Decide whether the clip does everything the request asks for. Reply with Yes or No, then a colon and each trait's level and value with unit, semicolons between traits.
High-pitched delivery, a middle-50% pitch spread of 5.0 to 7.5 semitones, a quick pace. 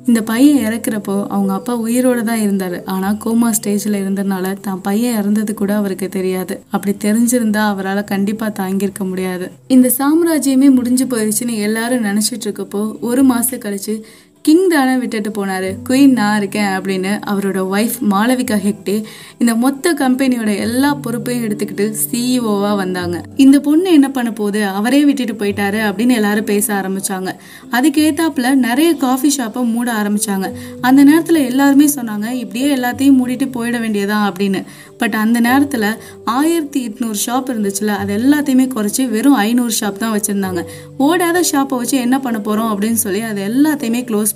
No: high, 225 Hz; average, 4.0 semitones; fast, 145 wpm